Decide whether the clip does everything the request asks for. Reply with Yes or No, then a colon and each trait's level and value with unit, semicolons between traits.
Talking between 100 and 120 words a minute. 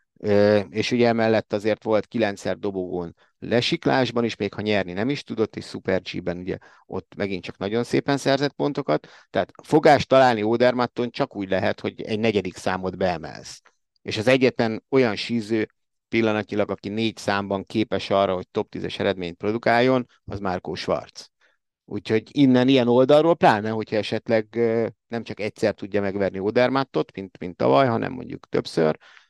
No: fast, 155 wpm